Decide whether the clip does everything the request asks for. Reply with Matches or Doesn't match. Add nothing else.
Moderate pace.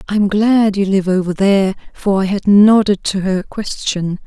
Matches